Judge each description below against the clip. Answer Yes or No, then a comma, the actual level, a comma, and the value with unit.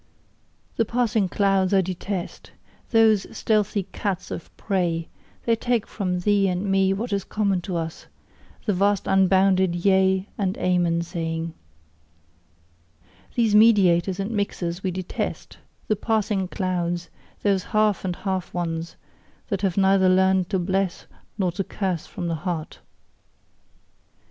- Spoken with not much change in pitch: Yes, narrow, 2.2 semitones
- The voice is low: No, high, 190 Hz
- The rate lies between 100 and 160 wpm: Yes, slow, 135 wpm